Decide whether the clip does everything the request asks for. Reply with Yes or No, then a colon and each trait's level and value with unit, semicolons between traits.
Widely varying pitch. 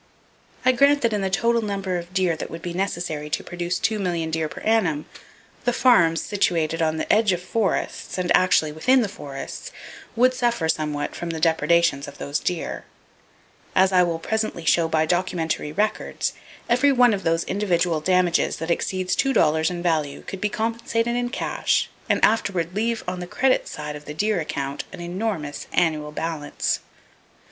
No: average, 4.8 semitones